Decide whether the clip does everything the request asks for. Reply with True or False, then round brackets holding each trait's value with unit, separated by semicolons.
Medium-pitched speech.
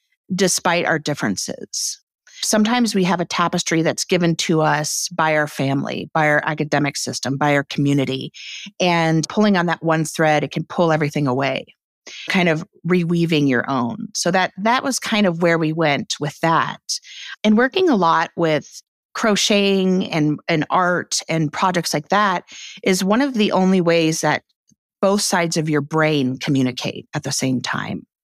True (165 Hz)